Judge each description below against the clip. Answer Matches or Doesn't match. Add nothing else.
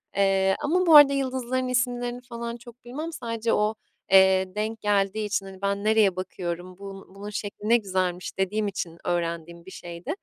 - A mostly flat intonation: Doesn't match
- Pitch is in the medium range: Doesn't match